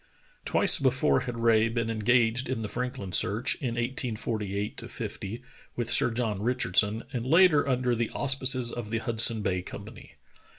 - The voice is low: Yes, low, 115 Hz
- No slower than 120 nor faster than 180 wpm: Yes, average, 155 wpm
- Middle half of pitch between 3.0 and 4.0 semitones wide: No, narrow, 2.5 semitones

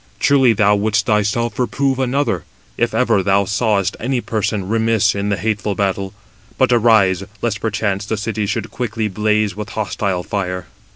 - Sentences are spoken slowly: No, average, 160 wpm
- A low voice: Yes, low, 105 Hz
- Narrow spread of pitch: Yes, narrow, 2.3 semitones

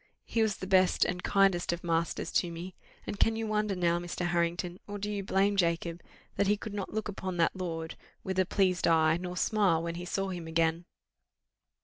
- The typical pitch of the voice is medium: Yes, medium, 180 Hz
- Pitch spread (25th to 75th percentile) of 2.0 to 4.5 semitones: Yes, average, 2.7 semitones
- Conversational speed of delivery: No, fast, 210 wpm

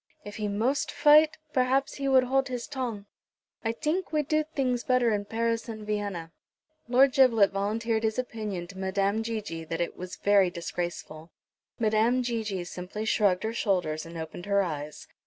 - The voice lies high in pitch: Yes, high, 220 Hz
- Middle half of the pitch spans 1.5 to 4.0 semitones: No, average, 4.8 semitones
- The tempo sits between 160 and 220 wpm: Yes, average, 170 wpm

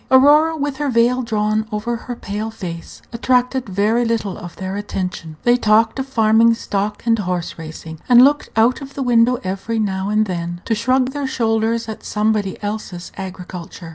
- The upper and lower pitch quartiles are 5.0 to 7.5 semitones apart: No, average, 3.9 semitones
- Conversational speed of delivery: Yes, average, 175 wpm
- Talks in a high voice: Yes, high, 220 Hz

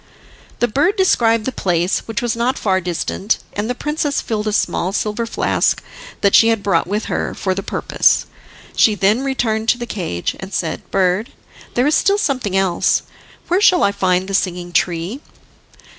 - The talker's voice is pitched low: No, high, 210 Hz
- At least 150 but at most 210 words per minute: Yes, average, 180 wpm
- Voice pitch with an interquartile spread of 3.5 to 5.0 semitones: Yes, average, 4.4 semitones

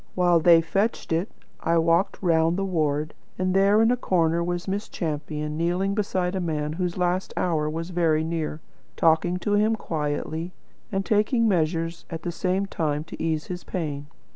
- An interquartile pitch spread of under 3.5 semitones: Yes, average, 2.8 semitones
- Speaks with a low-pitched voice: No, medium, 170 Hz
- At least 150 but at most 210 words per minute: Yes, average, 175 wpm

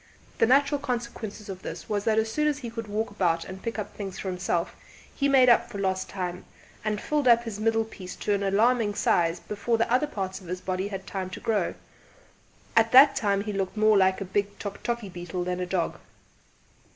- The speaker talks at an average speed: No, fast, 220 wpm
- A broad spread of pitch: No, average, 3.4 semitones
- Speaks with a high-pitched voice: Yes, high, 205 Hz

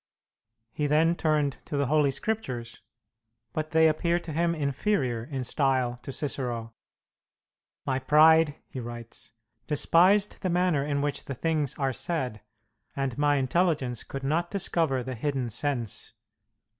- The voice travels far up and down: No, average, 3.8 semitones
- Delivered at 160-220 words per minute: No, average, 140 wpm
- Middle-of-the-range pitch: Yes, medium, 145 Hz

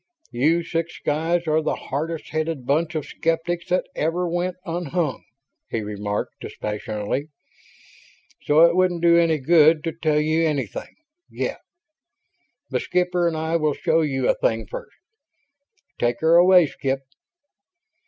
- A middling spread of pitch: Yes, average, 3.0 semitones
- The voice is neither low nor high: Yes, medium, 160 Hz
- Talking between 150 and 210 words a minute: No, average, 140 wpm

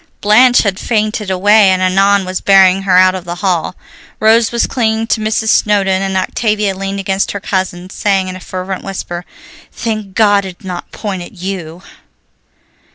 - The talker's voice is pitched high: Yes, high, 195 Hz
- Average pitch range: No, narrow, 2.2 semitones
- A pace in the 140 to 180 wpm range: Yes, average, 175 wpm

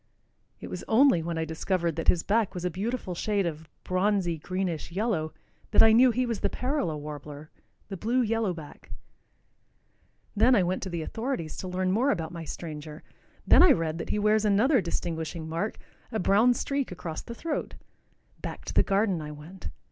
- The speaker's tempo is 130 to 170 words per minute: No, average, 185 wpm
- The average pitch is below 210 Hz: Yes, medium, 185 Hz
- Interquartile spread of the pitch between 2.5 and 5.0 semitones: No, wide, 5.4 semitones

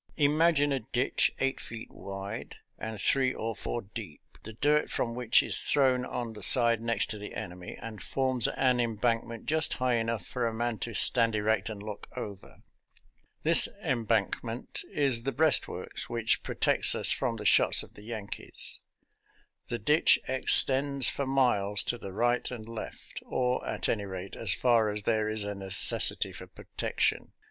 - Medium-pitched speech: No, low, 115 Hz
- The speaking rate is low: No, average, 170 wpm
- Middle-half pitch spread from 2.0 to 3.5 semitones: Yes, average, 3.1 semitones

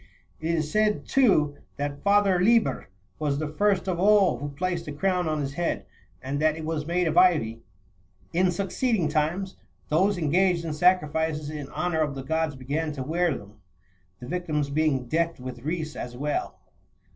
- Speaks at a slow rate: No, average, 175 wpm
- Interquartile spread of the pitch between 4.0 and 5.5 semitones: No, average, 3.6 semitones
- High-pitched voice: No, medium, 160 Hz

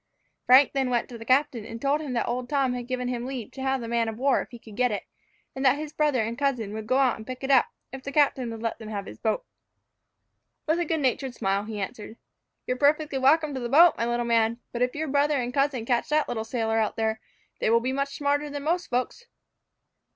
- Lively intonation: No, average, 3.4 semitones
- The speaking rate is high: Yes, fast, 255 wpm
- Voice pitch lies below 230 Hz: No, very high, 255 Hz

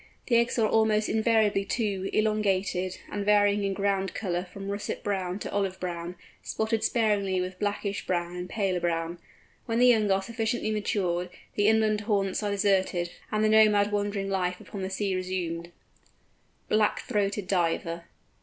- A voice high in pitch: Yes, high, 200 Hz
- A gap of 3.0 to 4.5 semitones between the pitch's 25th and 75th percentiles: No, narrow, 2.5 semitones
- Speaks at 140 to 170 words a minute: Yes, average, 160 wpm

